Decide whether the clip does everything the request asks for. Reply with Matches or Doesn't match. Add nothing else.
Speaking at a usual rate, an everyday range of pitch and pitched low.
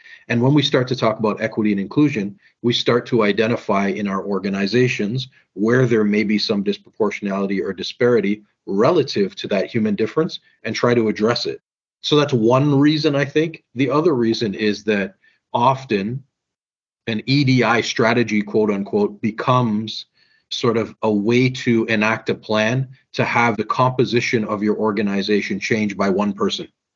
Matches